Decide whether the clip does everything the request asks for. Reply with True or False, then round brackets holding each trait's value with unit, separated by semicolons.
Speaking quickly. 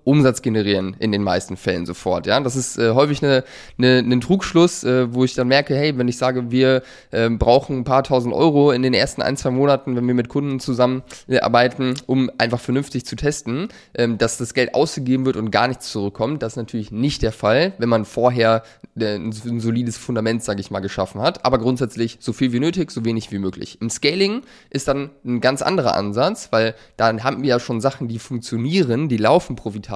True (210 wpm)